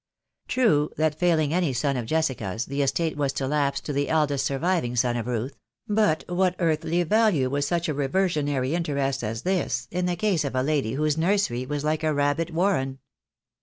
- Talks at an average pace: Yes, average, 195 wpm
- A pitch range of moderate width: Yes, average, 4.2 semitones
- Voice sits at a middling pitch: Yes, medium, 150 Hz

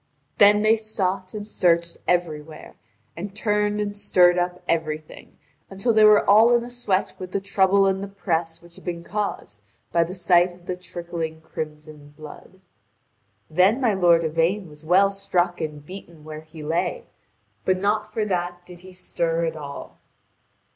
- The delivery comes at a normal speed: Yes, average, 170 wpm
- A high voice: No, medium, 180 Hz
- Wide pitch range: No, average, 3.3 semitones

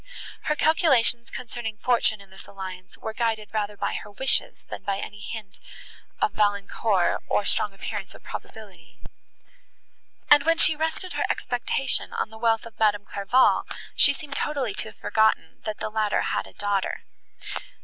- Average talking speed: Yes, average, 160 wpm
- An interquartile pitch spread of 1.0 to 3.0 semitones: No, average, 3.5 semitones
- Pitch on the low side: No, high, 220 Hz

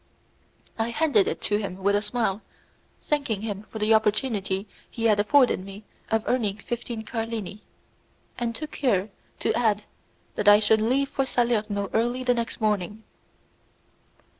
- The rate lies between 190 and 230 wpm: No, average, 150 wpm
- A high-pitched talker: Yes, high, 220 Hz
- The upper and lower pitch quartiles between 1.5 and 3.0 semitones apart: Yes, average, 2.7 semitones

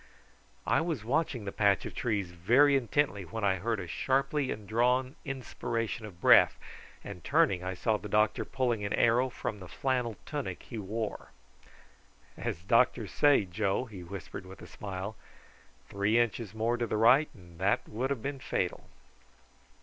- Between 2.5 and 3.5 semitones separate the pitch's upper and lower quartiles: No, average, 4.5 semitones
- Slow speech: No, average, 165 wpm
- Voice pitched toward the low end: Yes, low, 110 Hz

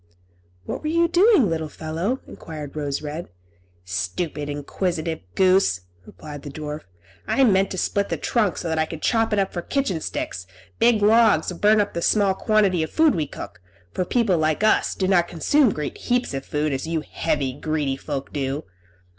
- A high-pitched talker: No, medium, 170 Hz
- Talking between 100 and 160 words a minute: No, average, 190 wpm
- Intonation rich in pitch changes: Yes, wide, 5.8 semitones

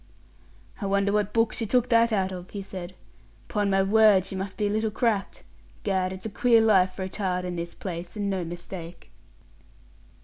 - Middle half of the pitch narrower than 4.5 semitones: Yes, narrow, 2.5 semitones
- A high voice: Yes, high, 195 Hz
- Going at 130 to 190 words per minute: No, average, 200 wpm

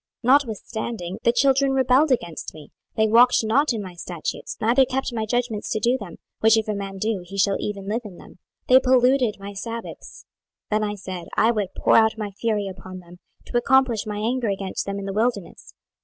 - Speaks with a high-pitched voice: Yes, high, 220 Hz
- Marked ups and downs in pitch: No, average, 3.7 semitones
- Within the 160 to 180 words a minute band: No, fast, 205 wpm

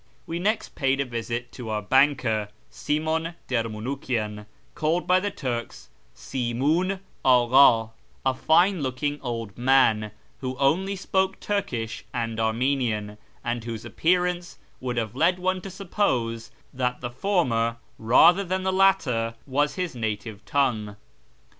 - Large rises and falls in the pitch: Yes, wide, 7.0 semitones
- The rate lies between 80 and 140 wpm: Yes, slow, 135 wpm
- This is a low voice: Yes, low, 130 Hz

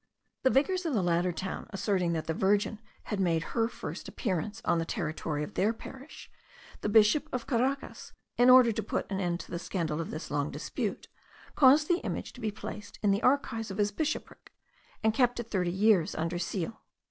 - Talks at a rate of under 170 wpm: No, average, 200 wpm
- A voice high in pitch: Yes, high, 205 Hz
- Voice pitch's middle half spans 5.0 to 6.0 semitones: Yes, wide, 5.6 semitones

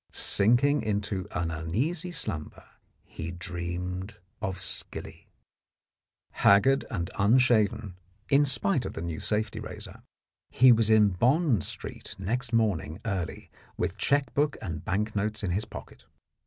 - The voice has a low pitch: Yes, low, 105 Hz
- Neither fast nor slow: No, slow, 130 wpm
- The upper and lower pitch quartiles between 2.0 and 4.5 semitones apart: No, average, 5.2 semitones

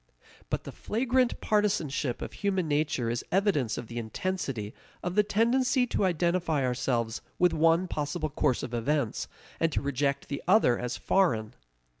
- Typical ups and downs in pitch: No, wide, 7.5 semitones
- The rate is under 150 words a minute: No, average, 155 wpm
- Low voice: No, medium, 155 Hz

